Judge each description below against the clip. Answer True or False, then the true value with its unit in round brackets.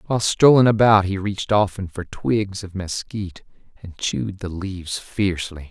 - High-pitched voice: False (95 Hz)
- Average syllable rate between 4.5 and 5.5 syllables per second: True (5.0 syllables/s)